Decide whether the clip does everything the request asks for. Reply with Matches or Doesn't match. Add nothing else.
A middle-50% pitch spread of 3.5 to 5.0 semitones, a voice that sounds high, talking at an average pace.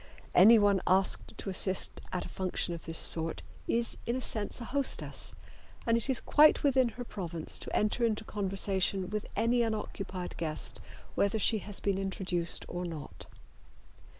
Matches